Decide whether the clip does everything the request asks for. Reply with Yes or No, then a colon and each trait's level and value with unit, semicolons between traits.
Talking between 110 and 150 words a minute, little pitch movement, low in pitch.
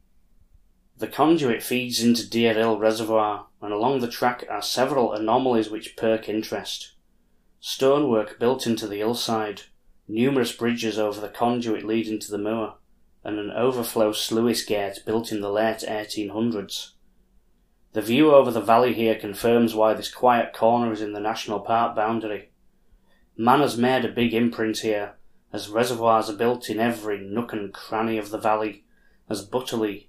No: average, 160 wpm; narrow, 1.8 semitones; low, 110 Hz